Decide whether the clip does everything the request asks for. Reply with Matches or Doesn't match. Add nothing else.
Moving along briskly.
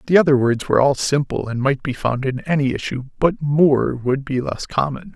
Matches